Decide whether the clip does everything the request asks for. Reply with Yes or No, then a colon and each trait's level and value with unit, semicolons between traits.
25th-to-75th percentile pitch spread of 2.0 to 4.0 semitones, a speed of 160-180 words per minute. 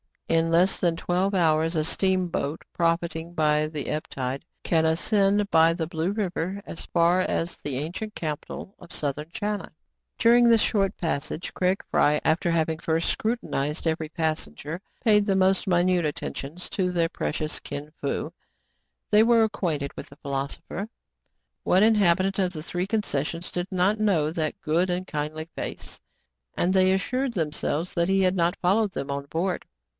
Yes: average, 3.5 semitones; average, 170 wpm